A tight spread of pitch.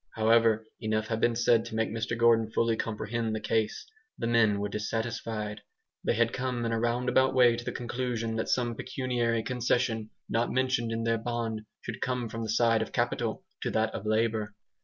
Yes: narrow, 1.3 semitones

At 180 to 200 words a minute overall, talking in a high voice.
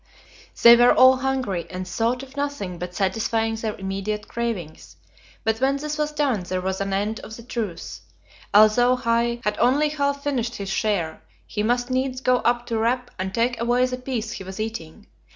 Yes: average, 190 wpm; high, 230 Hz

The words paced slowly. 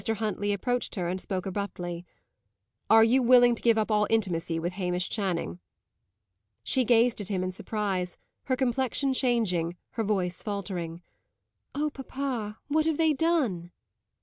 No: average, 150 wpm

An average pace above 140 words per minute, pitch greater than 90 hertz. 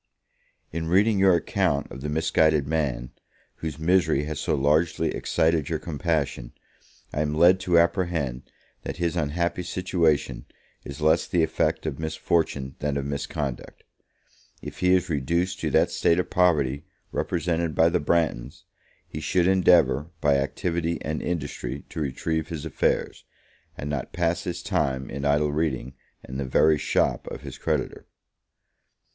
No: average, 150 wpm; very low, 80 Hz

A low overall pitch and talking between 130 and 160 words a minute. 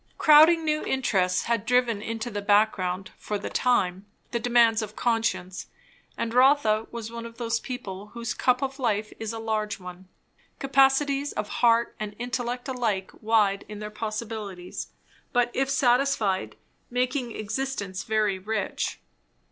No: high, 225 Hz; average, 145 wpm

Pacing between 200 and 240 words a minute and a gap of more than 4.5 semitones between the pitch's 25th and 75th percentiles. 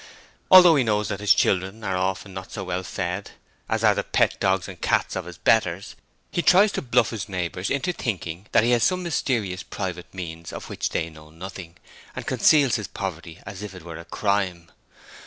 No: fast, 205 wpm; average, 3.8 semitones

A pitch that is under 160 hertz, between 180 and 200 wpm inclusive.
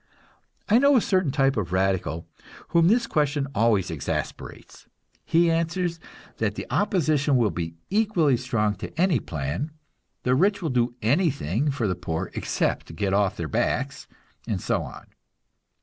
No: low, 135 Hz; average, 150 wpm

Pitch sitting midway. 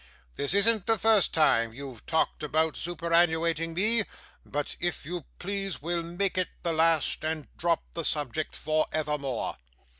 Yes: medium, 165 Hz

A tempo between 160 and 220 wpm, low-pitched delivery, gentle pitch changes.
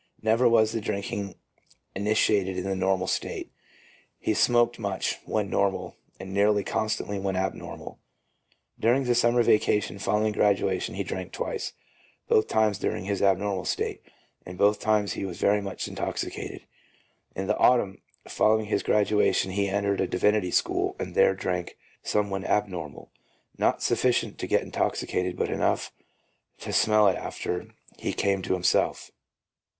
No: average, 150 wpm; low, 100 Hz; narrow, 2.0 semitones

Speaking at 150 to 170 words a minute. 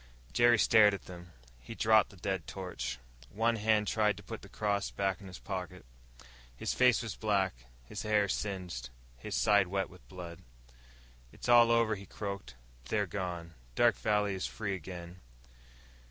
Yes: average, 165 wpm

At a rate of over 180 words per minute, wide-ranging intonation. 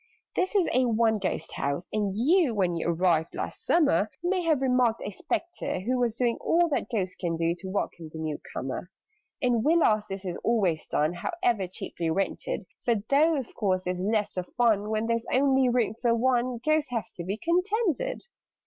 Yes: average, 195 wpm; wide, 6.2 semitones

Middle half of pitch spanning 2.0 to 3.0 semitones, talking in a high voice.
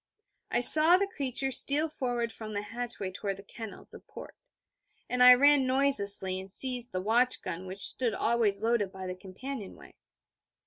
No: average, 4.7 semitones; high, 235 Hz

